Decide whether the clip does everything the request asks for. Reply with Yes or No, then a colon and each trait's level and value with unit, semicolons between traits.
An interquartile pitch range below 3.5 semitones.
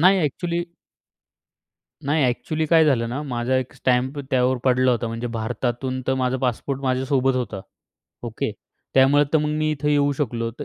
Yes: average, 2.9 semitones